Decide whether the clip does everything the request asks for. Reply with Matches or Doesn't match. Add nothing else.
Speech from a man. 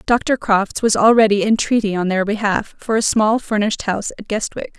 Doesn't match